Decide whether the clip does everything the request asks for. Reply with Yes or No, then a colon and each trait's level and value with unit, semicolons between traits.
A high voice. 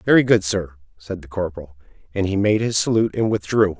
No: very low, 95 Hz